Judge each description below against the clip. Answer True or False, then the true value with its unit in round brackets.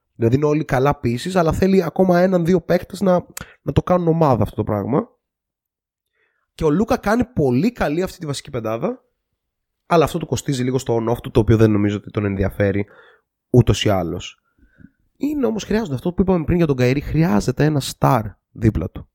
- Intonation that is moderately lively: False (7.8 semitones)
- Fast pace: True (190 wpm)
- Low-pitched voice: False (145 Hz)